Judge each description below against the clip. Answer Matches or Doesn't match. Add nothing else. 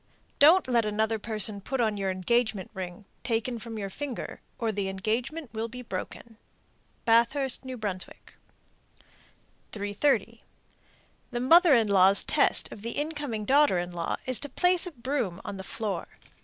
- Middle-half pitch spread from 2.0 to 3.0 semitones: Doesn't match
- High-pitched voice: Matches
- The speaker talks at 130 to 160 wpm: Matches